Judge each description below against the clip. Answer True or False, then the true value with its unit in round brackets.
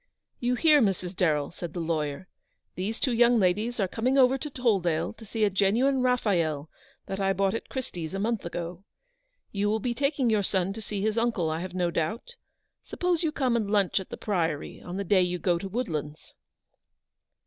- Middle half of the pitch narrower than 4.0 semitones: False (5.1 semitones)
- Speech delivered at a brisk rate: True (210 wpm)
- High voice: True (200 Hz)